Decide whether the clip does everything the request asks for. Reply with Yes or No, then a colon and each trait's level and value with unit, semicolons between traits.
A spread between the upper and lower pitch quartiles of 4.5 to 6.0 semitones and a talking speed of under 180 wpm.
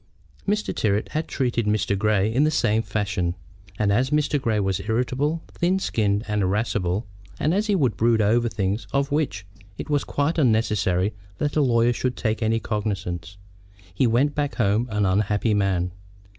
Yes: average, 5.1 semitones; average, 170 wpm